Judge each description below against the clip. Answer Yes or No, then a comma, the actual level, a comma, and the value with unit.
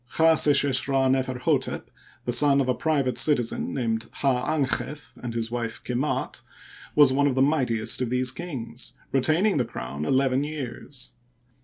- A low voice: Yes, low, 130 Hz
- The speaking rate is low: No, average, 150 wpm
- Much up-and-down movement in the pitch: No, average, 2.8 semitones